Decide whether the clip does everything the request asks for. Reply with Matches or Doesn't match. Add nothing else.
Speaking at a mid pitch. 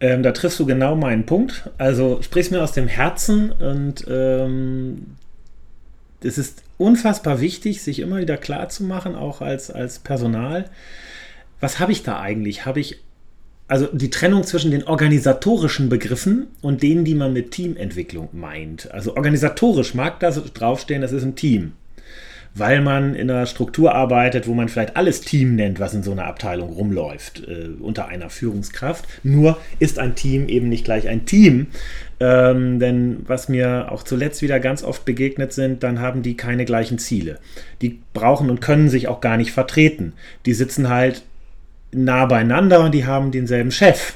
Doesn't match